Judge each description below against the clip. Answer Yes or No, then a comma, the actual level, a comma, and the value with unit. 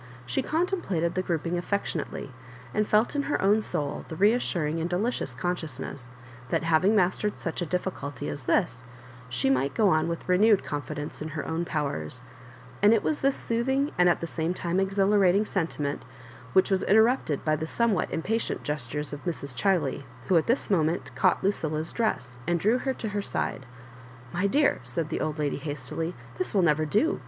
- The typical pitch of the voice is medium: Yes, medium, 175 Hz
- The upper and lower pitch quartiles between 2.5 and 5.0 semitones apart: No, wide, 5.5 semitones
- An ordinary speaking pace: Yes, average, 185 wpm